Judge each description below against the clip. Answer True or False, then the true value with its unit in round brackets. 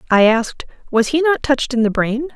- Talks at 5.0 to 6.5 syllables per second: True (6.0 syllables/s)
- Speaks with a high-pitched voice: True (255 Hz)